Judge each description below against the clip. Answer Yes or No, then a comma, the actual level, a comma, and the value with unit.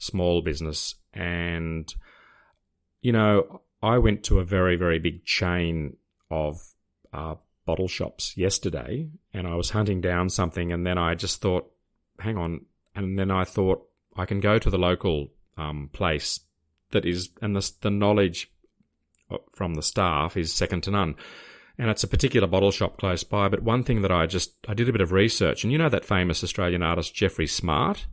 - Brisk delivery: No, average, 180 wpm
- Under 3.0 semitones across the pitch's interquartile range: No, average, 3.4 semitones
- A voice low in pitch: Yes, very low, 90 Hz